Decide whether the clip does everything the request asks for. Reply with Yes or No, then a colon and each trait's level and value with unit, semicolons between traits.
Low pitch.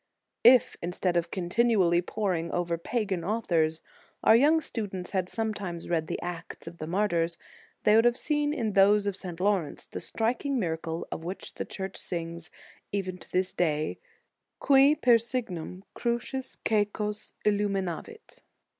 No: high, 195 Hz